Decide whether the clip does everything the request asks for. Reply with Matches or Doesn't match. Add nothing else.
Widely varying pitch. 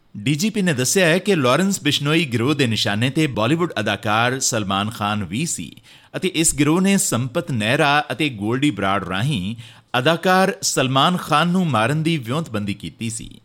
Matches